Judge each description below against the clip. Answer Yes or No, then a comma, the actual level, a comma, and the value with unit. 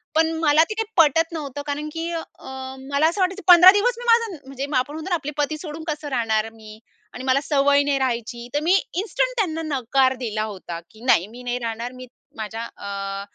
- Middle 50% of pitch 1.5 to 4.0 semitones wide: No, wide, 5.5 semitones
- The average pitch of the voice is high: Yes, very high, 285 Hz